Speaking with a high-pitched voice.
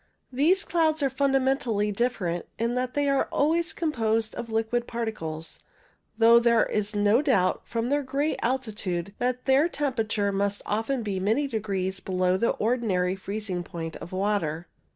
Yes: high, 225 Hz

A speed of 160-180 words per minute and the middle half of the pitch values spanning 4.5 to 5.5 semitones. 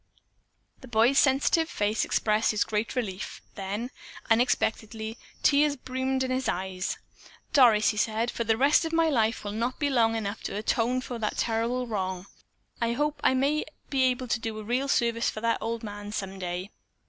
No: average, 175 wpm; average, 3.4 semitones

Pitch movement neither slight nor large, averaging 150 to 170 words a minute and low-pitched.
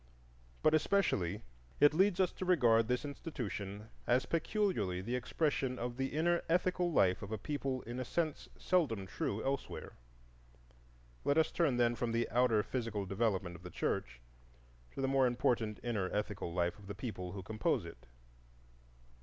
No: wide, 6.3 semitones; average, 160 wpm; low, 120 Hz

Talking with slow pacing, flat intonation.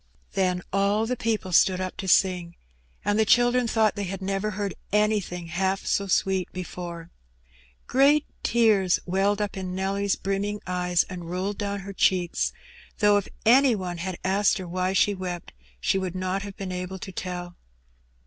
No: average, 170 wpm; narrow, 2.1 semitones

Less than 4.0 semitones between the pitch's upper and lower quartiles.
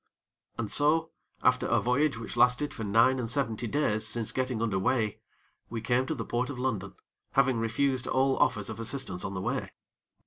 Yes: average, 3.0 semitones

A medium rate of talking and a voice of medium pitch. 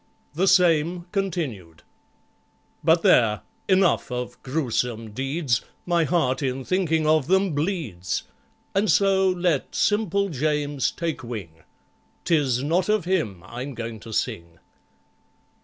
No: slow, 115 wpm; medium, 150 Hz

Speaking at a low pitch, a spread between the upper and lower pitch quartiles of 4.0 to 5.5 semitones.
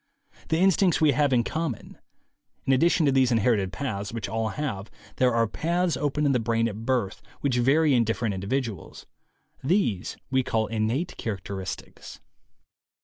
Yes: low, 125 Hz; average, 4.9 semitones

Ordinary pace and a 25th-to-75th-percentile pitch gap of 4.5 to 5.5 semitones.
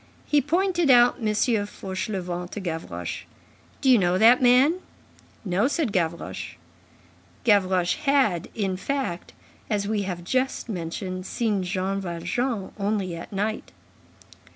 No: slow, 125 wpm; average, 5.2 semitones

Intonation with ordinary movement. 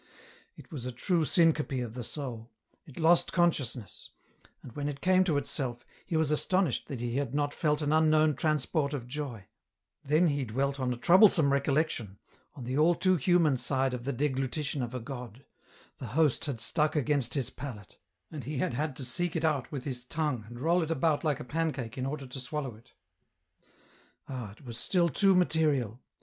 Yes: average, 3.9 semitones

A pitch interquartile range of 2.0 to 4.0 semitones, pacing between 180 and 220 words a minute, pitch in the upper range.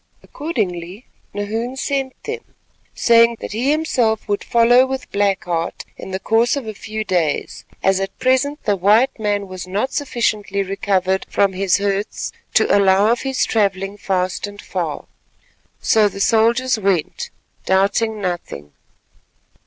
No: average, 3.6 semitones; average, 145 wpm; high, 205 Hz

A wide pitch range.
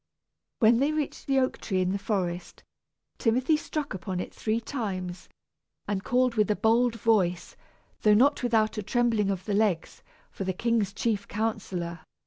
No: average, 3.8 semitones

